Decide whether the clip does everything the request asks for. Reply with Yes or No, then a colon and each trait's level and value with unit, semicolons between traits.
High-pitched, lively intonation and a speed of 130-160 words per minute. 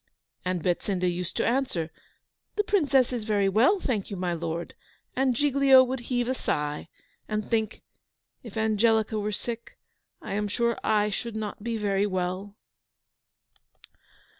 No: high, 215 Hz; average, 4.2 semitones; average, 145 wpm